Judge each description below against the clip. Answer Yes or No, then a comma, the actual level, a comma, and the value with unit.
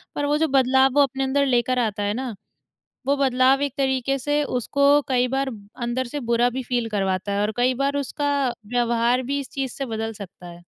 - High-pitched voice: Yes, very high, 255 Hz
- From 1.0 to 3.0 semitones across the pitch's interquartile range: Yes, average, 2.7 semitones